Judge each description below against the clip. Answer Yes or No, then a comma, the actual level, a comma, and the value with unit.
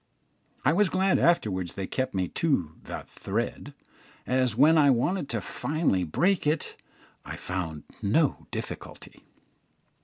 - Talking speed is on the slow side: Yes, slow, 130 wpm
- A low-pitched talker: Yes, low, 130 Hz